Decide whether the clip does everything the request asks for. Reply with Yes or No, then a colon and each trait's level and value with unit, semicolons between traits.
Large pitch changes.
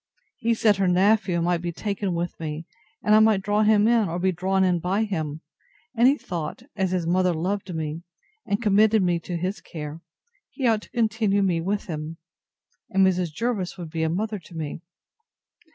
No: average, 3.7 semitones